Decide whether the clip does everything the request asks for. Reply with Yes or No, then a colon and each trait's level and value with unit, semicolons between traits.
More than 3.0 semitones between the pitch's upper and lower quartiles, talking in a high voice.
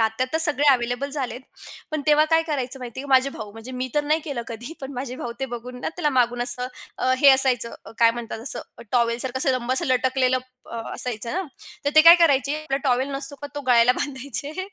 No: average, 2.7 semitones; very high, 260 Hz